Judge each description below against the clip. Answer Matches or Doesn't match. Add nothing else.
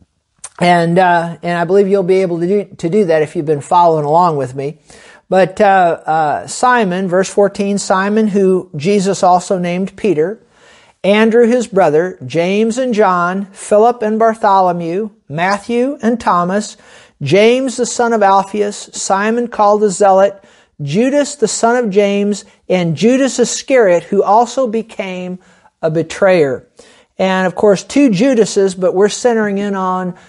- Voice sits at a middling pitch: Doesn't match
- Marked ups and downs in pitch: Doesn't match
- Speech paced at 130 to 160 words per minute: Matches